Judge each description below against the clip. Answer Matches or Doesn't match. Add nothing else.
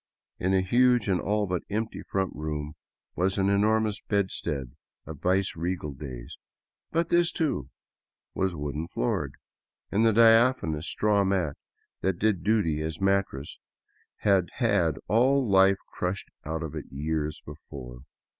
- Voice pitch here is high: Doesn't match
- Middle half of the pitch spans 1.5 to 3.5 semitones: Doesn't match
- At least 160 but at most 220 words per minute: Doesn't match